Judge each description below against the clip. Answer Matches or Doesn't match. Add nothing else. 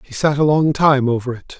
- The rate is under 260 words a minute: Doesn't match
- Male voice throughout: Matches